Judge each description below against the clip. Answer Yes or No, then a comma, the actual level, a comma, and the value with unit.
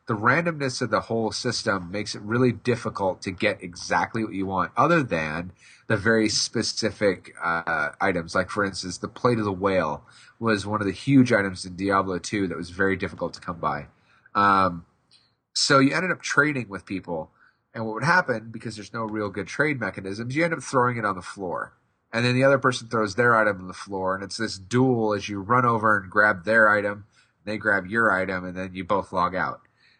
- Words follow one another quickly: Yes, fast, 215 wpm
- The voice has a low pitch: Yes, low, 105 Hz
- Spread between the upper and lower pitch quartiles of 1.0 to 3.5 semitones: No, average, 4.0 semitones